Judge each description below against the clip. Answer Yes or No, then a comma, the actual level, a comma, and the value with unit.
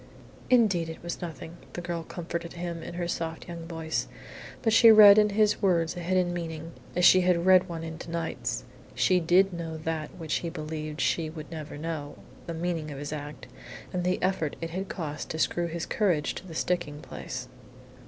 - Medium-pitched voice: Yes, medium, 170 Hz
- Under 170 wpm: No, average, 195 wpm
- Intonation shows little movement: Yes, narrow, 1.9 semitones